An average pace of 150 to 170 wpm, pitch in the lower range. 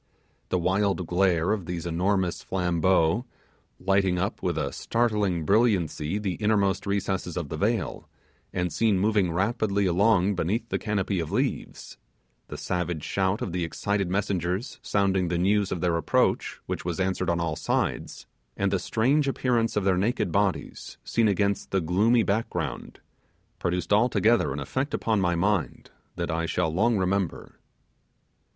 Yes: average, 155 wpm; very low, 95 Hz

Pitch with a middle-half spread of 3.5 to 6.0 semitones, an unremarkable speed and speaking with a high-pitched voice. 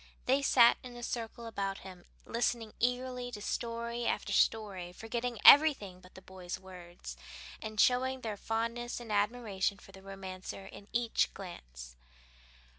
Yes: average, 4.1 semitones; average, 145 wpm; high, 220 Hz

